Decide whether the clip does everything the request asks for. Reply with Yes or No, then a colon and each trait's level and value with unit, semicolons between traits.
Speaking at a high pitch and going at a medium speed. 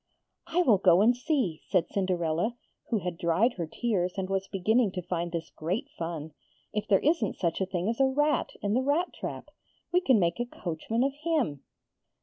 Yes: high, 200 Hz; average, 195 wpm